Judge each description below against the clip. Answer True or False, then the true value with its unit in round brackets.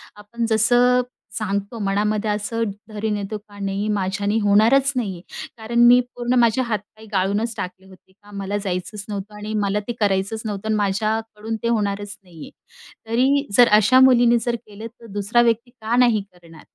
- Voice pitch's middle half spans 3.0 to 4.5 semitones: False (2.6 semitones)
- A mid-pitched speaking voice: False (215 Hz)